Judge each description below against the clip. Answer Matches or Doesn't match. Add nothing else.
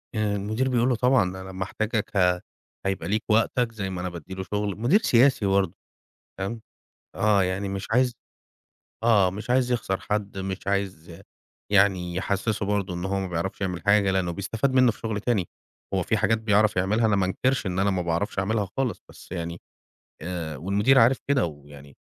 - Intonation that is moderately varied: Matches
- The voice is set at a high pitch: Doesn't match